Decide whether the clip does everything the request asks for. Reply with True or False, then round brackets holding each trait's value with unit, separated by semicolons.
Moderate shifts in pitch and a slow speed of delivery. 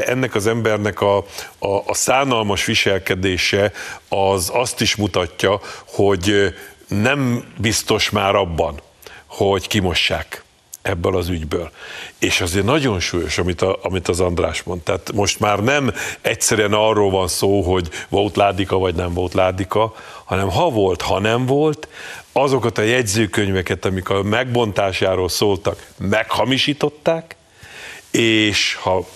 False (3.2 semitones; 130 wpm)